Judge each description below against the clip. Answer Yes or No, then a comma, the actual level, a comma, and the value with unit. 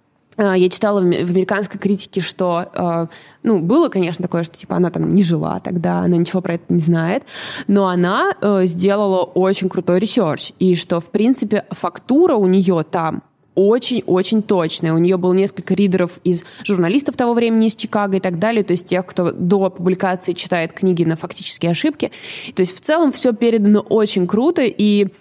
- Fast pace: Yes, fast, 175 wpm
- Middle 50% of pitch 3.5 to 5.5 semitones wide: No, average, 2.9 semitones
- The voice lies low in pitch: No, high, 190 Hz